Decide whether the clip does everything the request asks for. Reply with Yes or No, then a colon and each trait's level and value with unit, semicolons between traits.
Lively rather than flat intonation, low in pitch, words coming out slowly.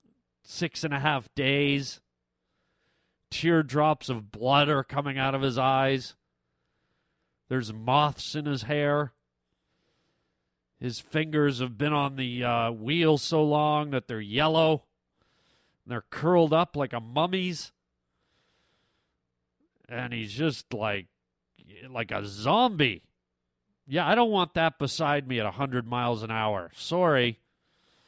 Yes: wide, 5.7 semitones; low, 130 Hz; slow, 125 wpm